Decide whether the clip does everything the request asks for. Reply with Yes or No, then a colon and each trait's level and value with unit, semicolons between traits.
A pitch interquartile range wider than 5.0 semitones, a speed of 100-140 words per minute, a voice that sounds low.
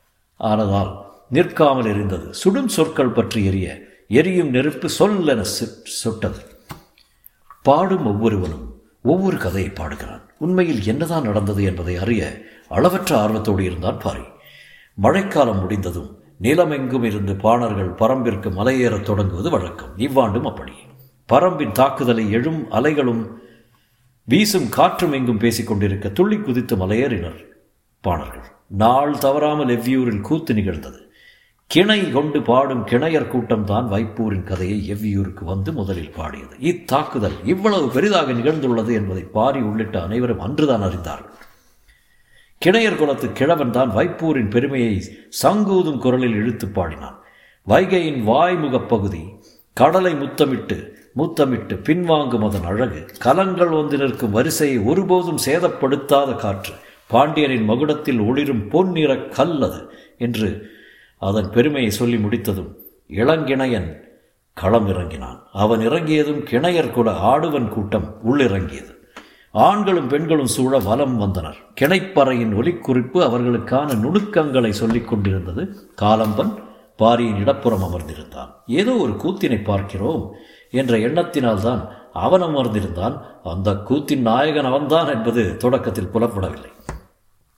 Yes: wide, 5.5 semitones; average, 105 wpm; low, 115 Hz